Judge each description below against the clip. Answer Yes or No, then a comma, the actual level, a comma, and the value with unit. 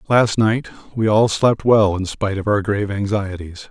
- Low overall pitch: Yes, low, 105 Hz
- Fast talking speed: No, average, 195 wpm